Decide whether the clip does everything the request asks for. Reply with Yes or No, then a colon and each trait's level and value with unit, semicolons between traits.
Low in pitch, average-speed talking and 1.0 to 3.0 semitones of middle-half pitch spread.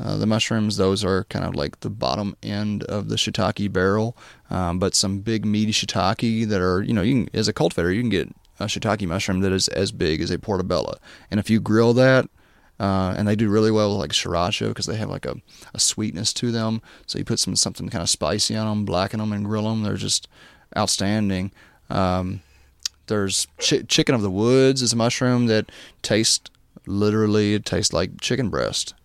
No: low, 105 Hz; fast, 210 wpm; average, 2.7 semitones